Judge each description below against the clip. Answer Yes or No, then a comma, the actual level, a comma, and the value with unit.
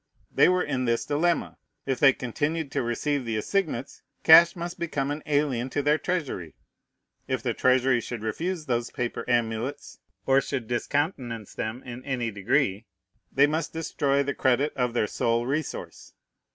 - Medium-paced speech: Yes, average, 160 wpm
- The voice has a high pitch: No, low, 135 Hz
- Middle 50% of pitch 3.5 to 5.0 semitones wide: Yes, average, 3.9 semitones